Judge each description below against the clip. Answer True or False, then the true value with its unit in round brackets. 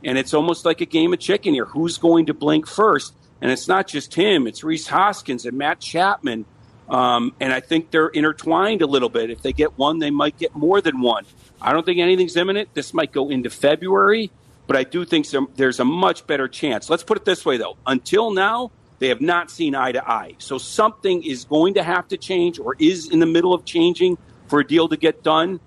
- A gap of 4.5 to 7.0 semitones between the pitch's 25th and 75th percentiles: True (5.3 semitones)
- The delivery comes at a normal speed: False (235 wpm)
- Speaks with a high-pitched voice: False (160 Hz)